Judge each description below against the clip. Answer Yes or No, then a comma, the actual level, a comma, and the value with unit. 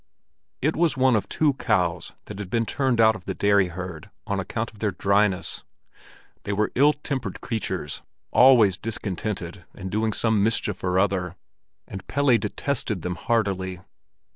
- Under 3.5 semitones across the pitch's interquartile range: No, average, 3.8 semitones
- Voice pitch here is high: No, low, 105 Hz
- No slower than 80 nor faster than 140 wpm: No, average, 160 wpm